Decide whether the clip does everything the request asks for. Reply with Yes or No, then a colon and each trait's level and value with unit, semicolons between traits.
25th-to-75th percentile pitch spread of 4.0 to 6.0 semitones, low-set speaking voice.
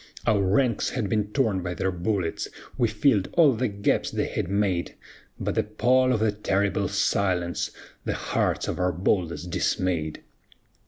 No: average, 3.5 semitones; low, 100 Hz